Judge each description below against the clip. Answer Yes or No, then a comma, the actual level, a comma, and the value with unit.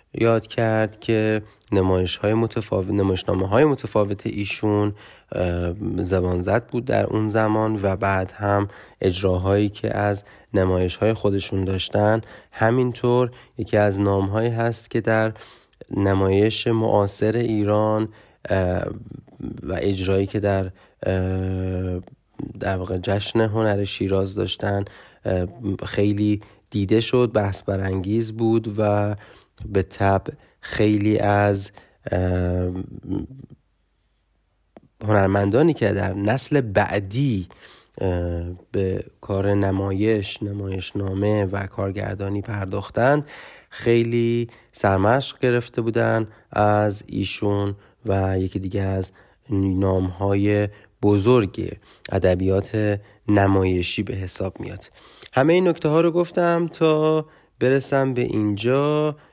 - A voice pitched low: Yes, low, 105 Hz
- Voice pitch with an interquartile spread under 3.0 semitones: Yes, narrow, 2.6 semitones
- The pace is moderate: No, slow, 100 wpm